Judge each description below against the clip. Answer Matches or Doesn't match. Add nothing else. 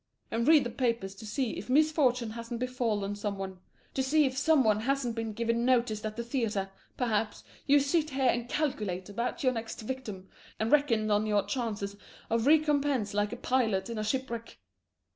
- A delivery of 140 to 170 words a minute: Doesn't match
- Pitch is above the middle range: Matches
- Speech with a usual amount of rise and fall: Matches